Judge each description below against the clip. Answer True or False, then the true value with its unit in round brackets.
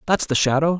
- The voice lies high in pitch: False (160 Hz)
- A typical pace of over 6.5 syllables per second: False (6.4 syllables/s)